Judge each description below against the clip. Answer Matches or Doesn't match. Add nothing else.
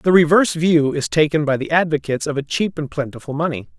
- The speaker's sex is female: Doesn't match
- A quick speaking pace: Matches